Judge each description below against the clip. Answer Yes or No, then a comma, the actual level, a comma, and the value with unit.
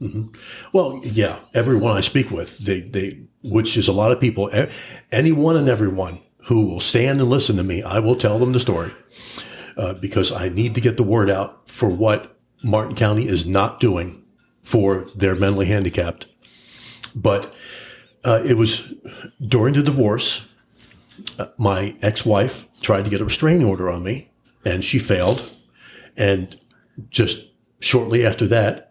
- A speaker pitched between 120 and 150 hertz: No, low, 110 Hz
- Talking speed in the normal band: Yes, average, 160 wpm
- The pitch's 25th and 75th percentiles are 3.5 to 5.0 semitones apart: Yes, average, 4.1 semitones